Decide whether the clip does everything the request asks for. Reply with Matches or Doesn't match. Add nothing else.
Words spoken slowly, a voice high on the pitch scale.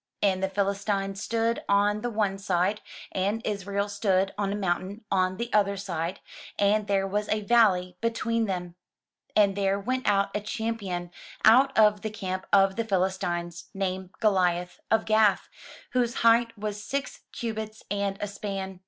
Doesn't match